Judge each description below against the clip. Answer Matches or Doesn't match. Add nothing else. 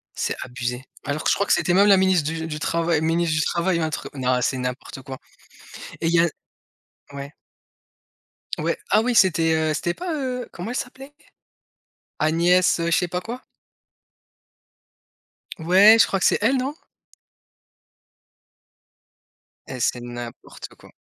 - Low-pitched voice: Doesn't match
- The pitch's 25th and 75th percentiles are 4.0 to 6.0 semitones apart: Matches